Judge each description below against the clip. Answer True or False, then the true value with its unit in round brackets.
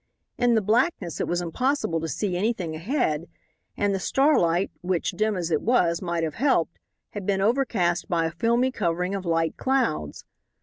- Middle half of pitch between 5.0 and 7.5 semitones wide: True (5.6 semitones)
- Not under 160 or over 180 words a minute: True (175 wpm)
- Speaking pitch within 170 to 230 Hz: True (185 Hz)